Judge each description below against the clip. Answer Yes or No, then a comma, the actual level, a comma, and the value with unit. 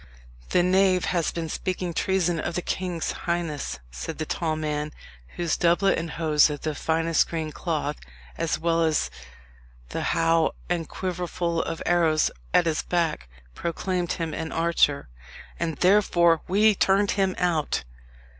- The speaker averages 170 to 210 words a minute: No, average, 145 wpm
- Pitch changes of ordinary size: No, narrow, 2.0 semitones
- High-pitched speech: No, medium, 170 Hz